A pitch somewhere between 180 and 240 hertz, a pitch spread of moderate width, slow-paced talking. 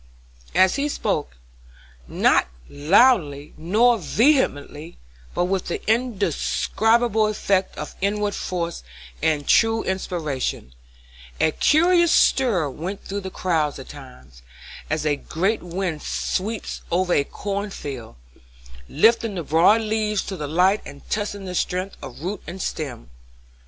No: medium, 185 Hz; wide, 5.7 semitones; slow, 130 wpm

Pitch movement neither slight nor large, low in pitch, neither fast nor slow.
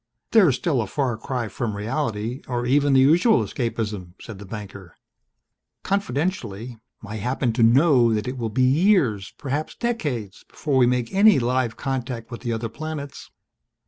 Yes: average, 4.2 semitones; low, 125 Hz; average, 160 wpm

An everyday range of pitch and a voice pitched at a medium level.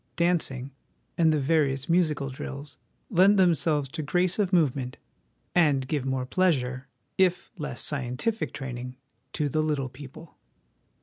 Yes: average, 4.3 semitones; medium, 150 Hz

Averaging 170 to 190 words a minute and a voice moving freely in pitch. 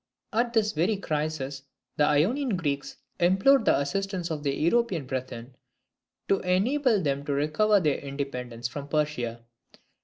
No: average, 140 wpm; wide, 6.1 semitones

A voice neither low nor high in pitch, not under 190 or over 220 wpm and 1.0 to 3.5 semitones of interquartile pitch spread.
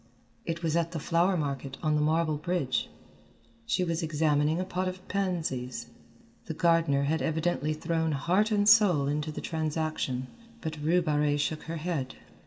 No: medium, 160 Hz; average, 165 wpm; narrow, 2.6 semitones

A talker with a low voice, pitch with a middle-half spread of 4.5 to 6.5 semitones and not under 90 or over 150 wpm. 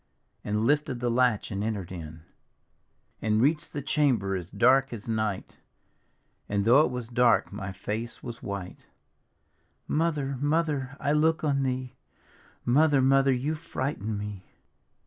Yes: low, 125 Hz; average, 5.1 semitones; average, 140 wpm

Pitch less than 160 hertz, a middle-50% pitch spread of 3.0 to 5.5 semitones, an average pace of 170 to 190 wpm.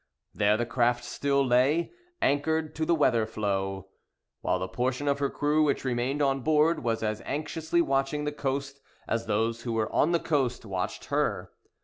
Yes: low, 135 Hz; average, 4.4 semitones; average, 175 wpm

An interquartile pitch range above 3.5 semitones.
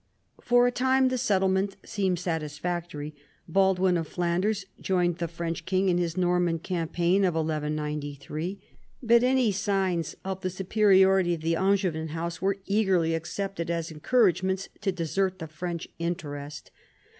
No: average, 2.8 semitones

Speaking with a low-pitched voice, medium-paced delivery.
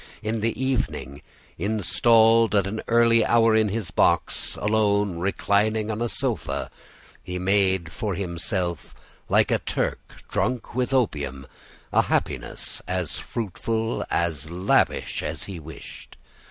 No: low, 105 Hz; slow, 125 wpm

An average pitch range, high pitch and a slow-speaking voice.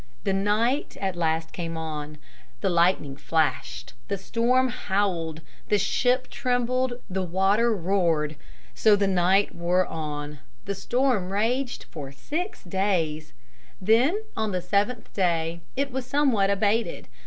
No: wide, 5.8 semitones; high, 195 Hz; slow, 130 wpm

